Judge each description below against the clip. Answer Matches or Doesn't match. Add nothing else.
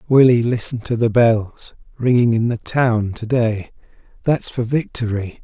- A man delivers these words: Matches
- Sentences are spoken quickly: Doesn't match